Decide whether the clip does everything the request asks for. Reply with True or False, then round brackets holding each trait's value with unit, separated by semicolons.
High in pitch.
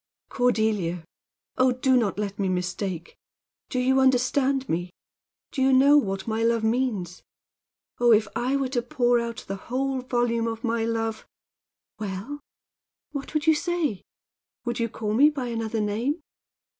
True (235 Hz)